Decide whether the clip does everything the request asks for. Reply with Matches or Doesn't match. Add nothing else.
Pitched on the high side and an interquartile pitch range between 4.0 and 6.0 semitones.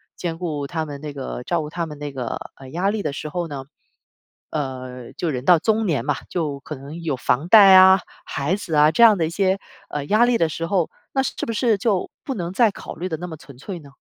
Doesn't match